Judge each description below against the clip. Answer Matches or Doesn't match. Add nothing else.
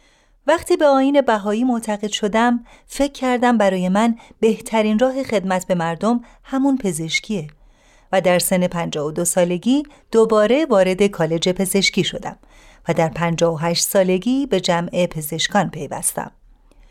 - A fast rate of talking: Doesn't match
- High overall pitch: Matches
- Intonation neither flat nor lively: Doesn't match